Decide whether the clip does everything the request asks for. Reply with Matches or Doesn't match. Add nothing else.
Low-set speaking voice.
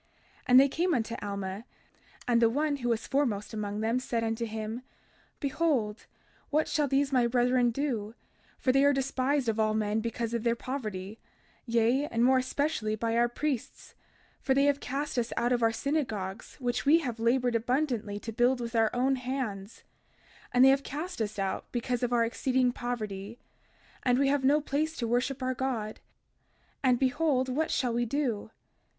Doesn't match